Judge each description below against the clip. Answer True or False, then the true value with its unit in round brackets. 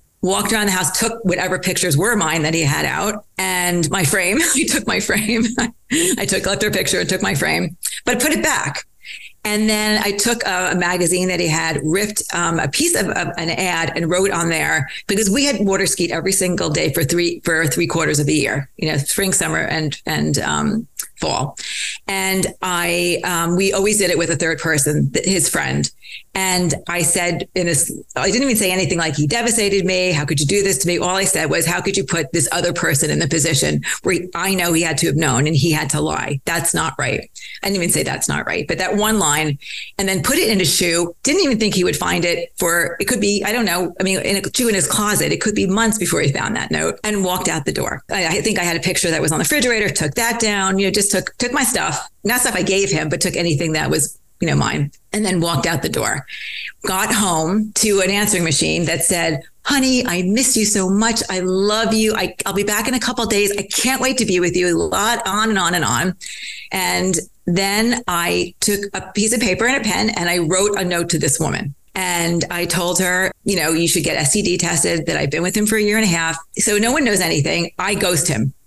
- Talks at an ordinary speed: False (250 wpm)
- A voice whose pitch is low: False (185 Hz)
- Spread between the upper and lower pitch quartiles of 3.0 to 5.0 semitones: True (3.8 semitones)